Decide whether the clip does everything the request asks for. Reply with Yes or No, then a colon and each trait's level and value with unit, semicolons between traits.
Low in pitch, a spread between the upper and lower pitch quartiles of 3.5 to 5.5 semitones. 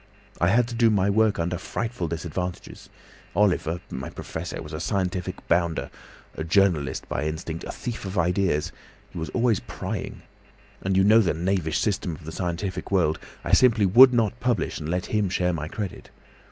Yes: very low, 90 Hz; average, 4.0 semitones